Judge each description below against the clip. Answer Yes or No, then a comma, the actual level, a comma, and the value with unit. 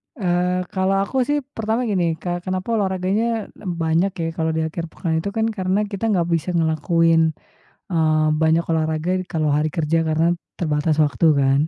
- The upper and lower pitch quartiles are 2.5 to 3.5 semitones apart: Yes, average, 3.1 semitones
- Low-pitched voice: No, medium, 170 Hz